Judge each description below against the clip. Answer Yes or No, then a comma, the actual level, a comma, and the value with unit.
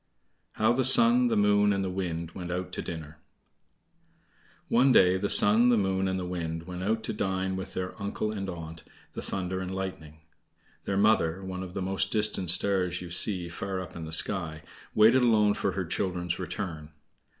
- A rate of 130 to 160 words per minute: No, average, 190 wpm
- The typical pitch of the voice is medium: No, very low, 95 Hz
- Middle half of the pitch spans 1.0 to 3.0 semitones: Yes, narrow, 2.6 semitones